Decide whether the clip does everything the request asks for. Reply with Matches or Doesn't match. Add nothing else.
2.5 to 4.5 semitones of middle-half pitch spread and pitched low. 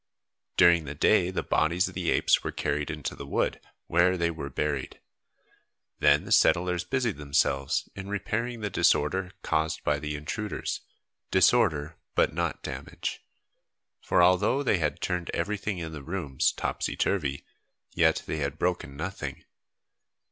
Matches